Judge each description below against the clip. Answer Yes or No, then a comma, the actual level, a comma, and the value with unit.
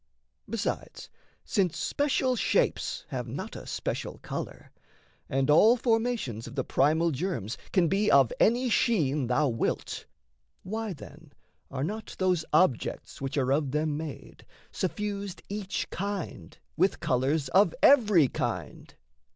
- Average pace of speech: No, slow, 130 wpm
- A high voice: No, medium, 165 Hz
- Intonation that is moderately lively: No, wide, 7.1 semitones